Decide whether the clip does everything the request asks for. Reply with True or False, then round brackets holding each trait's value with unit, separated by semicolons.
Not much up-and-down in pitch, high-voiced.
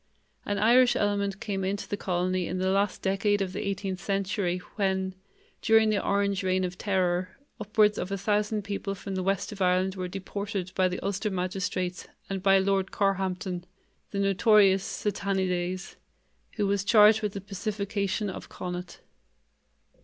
True (1.6 semitones; 195 Hz)